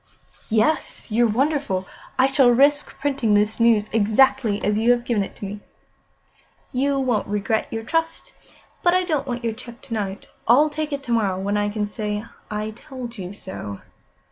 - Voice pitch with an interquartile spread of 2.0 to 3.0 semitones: No, average, 4.5 semitones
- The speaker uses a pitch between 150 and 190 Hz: No, high, 230 Hz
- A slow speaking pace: No, average, 180 wpm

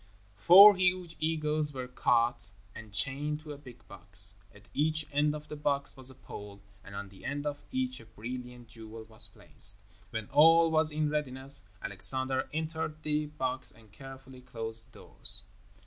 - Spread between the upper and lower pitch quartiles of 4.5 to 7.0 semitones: Yes, average, 5.1 semitones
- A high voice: No, low, 135 Hz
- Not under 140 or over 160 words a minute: No, average, 170 wpm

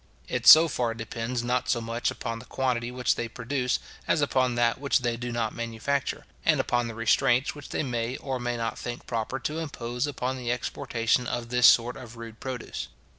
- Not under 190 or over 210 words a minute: Yes, average, 200 wpm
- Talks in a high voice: No, low, 120 Hz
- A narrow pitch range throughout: Yes, narrow, 1.5 semitones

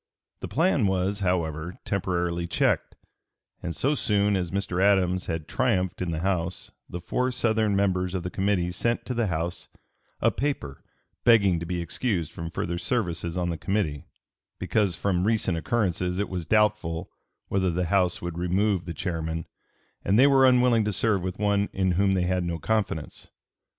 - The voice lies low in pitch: Yes, very low, 95 Hz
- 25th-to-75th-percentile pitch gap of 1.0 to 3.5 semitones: Yes, average, 3.2 semitones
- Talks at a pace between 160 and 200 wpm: Yes, average, 170 wpm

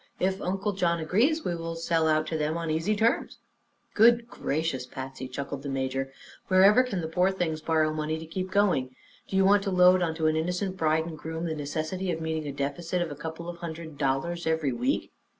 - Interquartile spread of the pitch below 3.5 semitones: Yes, average, 3.1 semitones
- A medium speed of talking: No, fast, 210 wpm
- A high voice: No, medium, 165 Hz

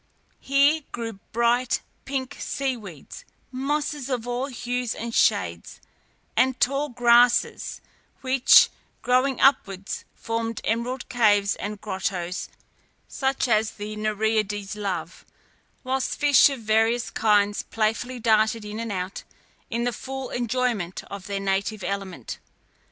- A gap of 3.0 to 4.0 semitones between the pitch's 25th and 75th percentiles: Yes, average, 3.6 semitones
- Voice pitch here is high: Yes, high, 230 Hz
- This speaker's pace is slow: Yes, slow, 120 wpm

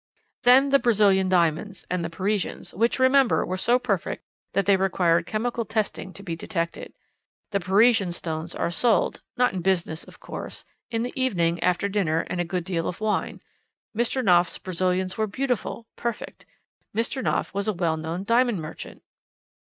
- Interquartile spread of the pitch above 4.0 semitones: Yes, average, 4.9 semitones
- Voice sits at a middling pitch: No, high, 195 Hz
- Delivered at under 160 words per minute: No, average, 165 wpm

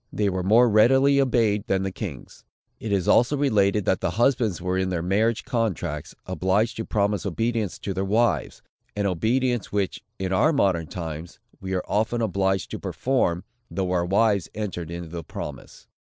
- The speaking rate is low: No, average, 175 wpm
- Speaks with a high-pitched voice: No, low, 100 Hz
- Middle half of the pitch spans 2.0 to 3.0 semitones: No, average, 3.6 semitones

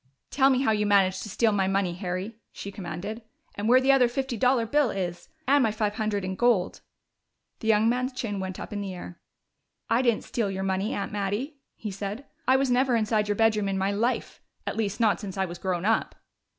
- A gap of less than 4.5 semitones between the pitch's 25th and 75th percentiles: Yes, average, 3.6 semitones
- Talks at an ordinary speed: No, fast, 225 wpm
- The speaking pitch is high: Yes, high, 210 Hz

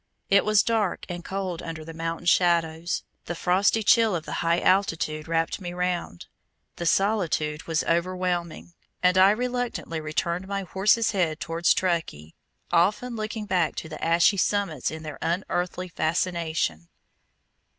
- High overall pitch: No, medium, 175 Hz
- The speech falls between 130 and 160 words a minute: Yes, average, 145 wpm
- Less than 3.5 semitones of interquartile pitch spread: Yes, average, 3.0 semitones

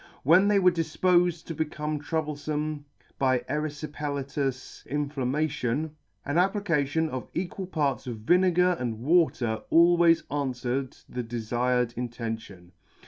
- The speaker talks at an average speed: No, slow, 110 wpm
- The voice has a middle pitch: Yes, medium, 150 Hz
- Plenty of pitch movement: No, average, 4.7 semitones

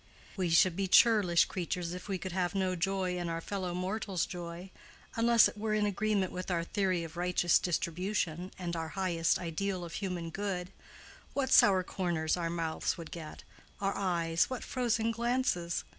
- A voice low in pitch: No, medium, 180 Hz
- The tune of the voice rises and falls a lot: No, narrow, 2.6 semitones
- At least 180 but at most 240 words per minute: No, average, 170 wpm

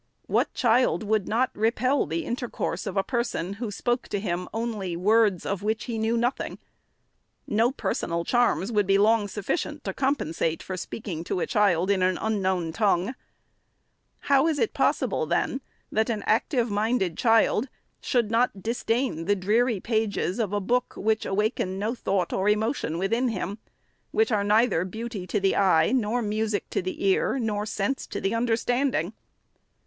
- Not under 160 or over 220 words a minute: Yes, average, 170 wpm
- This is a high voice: Yes, high, 215 Hz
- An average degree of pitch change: Yes, average, 3.6 semitones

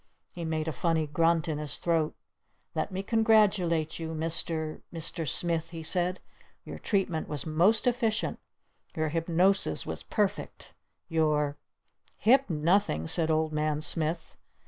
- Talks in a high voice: No, medium, 165 Hz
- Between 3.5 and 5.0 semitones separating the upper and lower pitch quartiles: No, average, 2.7 semitones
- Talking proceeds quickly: No, average, 140 wpm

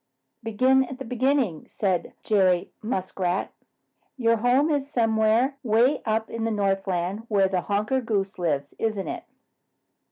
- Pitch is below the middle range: No, high, 220 Hz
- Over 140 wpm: No, slow, 135 wpm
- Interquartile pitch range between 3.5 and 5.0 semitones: Yes, average, 4.3 semitones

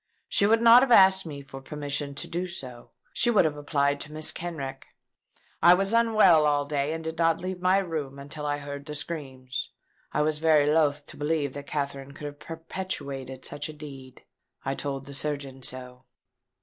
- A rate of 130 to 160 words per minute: No, average, 190 wpm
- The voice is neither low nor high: Yes, medium, 150 Hz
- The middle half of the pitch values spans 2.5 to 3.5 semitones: Yes, average, 2.8 semitones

